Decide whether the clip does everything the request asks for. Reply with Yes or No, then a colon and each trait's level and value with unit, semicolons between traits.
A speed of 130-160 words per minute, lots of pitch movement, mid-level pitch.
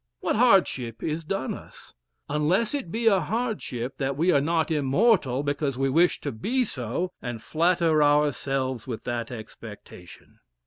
Yes: average, 150 wpm; wide, 5.7 semitones; medium, 150 Hz